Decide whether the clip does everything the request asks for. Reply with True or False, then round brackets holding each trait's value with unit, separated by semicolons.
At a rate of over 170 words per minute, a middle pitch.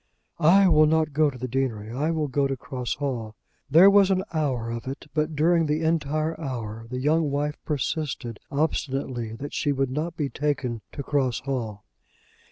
True (180 wpm; 145 Hz)